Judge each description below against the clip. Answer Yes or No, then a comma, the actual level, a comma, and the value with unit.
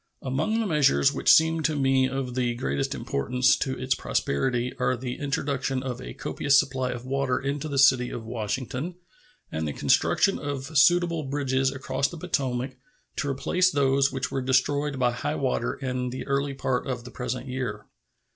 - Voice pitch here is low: Yes, low, 130 Hz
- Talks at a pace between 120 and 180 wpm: Yes, average, 175 wpm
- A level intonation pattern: Yes, narrow, 2.0 semitones